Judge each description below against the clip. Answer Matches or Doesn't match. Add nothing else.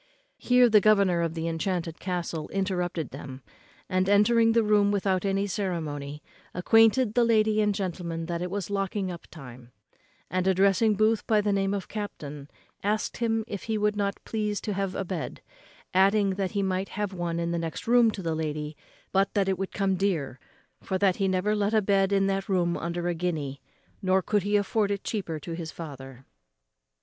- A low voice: Doesn't match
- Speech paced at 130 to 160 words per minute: Doesn't match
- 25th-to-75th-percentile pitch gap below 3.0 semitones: Doesn't match